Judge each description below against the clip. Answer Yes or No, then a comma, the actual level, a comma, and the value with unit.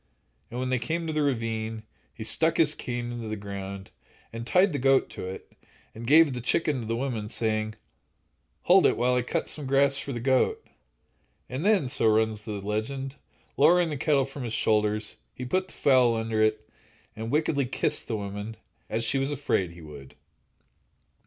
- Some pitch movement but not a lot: Yes, average, 4.2 semitones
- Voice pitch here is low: Yes, low, 120 Hz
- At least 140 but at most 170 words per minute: No, average, 185 wpm